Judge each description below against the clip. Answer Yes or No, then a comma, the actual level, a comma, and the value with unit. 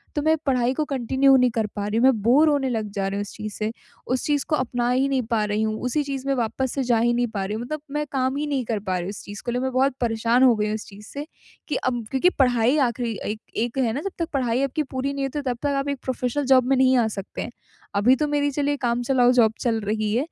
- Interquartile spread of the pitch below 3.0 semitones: No, average, 3.7 semitones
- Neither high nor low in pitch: No, very high, 250 Hz